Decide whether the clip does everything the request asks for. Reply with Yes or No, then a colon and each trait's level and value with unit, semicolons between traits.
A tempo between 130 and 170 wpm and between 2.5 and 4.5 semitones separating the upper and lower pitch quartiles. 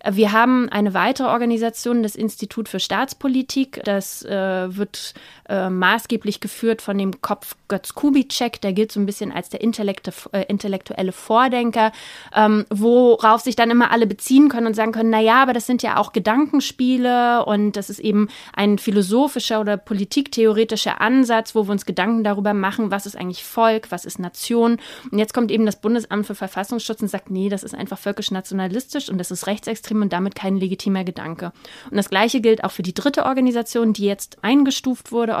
No: average, 180 wpm; average, 2.8 semitones